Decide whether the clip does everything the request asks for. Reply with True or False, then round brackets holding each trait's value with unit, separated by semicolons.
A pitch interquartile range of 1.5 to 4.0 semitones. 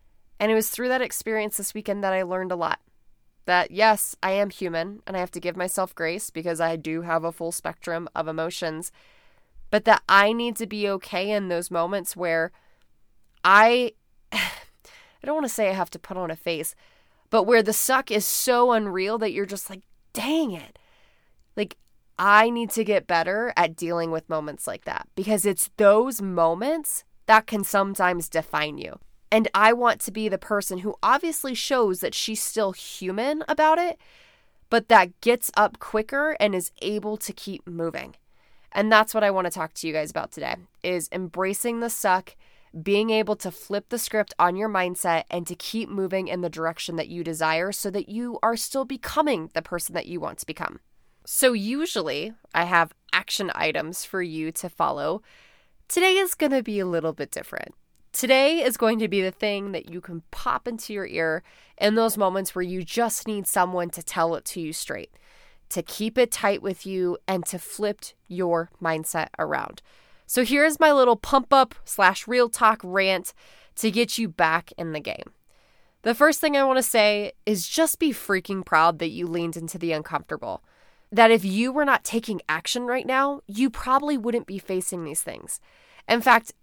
False (5.0 semitones)